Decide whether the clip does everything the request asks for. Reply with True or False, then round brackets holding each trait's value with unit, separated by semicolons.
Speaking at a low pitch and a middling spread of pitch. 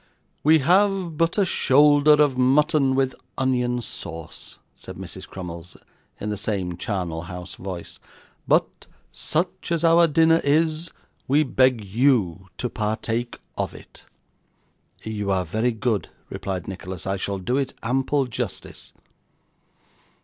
False (125 Hz; 7.3 semitones)